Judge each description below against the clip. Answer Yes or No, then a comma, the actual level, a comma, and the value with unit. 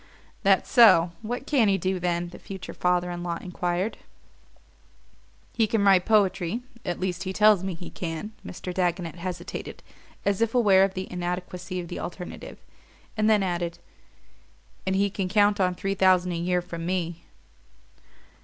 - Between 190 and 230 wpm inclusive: No, average, 165 wpm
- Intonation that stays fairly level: Yes, narrow, 2.1 semitones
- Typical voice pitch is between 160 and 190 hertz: Yes, medium, 185 Hz